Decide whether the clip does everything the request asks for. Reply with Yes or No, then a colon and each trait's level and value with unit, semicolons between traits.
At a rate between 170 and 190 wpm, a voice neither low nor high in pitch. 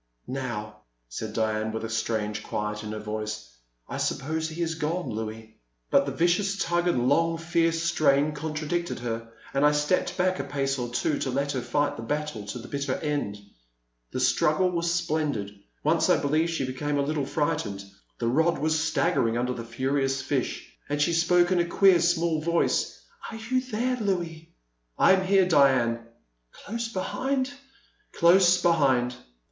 Yes: average, 180 wpm; medium, 150 Hz